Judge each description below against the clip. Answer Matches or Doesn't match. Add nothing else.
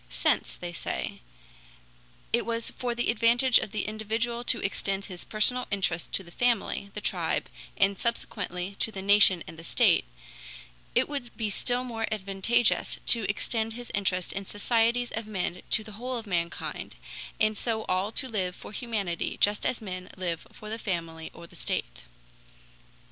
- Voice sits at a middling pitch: Doesn't match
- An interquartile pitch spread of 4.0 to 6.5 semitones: Doesn't match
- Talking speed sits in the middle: Matches